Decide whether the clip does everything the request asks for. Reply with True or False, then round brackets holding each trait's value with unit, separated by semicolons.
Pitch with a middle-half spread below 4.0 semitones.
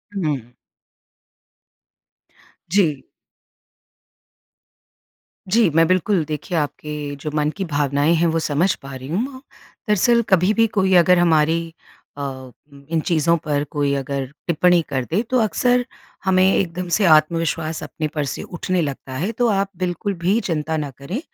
False (4.3 semitones)